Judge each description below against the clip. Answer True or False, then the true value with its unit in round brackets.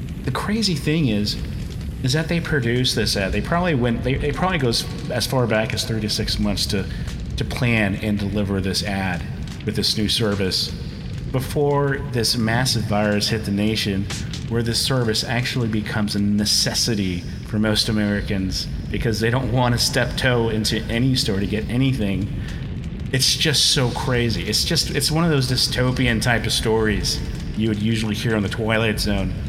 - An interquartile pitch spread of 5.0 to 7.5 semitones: False (3.7 semitones)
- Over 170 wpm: True (180 wpm)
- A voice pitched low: True (115 Hz)